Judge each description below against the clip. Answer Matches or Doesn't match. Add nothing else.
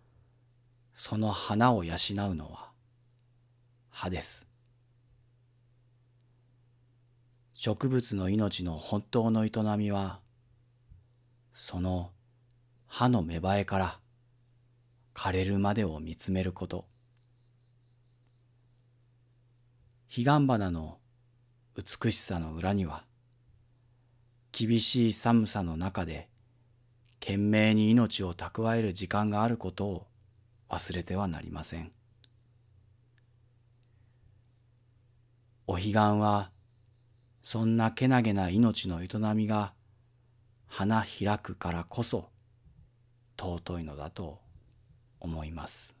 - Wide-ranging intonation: Doesn't match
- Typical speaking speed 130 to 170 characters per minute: Matches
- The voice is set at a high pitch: Doesn't match